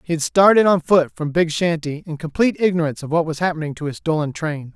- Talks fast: Yes, fast, 240 wpm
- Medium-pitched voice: Yes, medium, 165 Hz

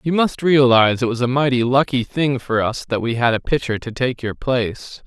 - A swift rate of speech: Yes, fast, 235 wpm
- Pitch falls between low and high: No, low, 125 Hz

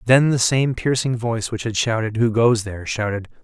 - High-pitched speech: No, low, 115 Hz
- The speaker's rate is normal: No, fast, 210 wpm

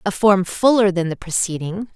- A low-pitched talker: No, high, 190 Hz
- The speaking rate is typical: Yes, average, 185 wpm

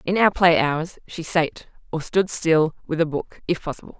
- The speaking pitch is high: No, medium, 165 Hz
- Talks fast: Yes, fast, 210 wpm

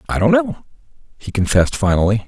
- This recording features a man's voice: Yes, male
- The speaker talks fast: No, average, 160 wpm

